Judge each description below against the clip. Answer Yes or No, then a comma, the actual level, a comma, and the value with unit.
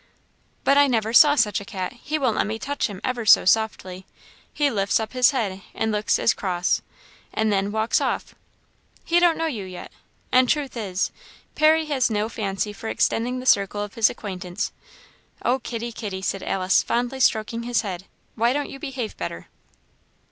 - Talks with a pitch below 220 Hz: No, high, 225 Hz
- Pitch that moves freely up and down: No, average, 4.4 semitones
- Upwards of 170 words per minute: Yes, average, 185 wpm